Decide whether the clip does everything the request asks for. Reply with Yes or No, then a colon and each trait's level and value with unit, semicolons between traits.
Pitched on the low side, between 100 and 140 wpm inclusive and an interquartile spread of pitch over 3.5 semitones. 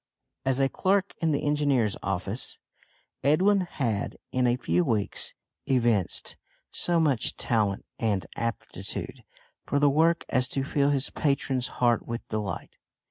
Yes: low, 130 Hz; slow, 135 wpm; average, 4.6 semitones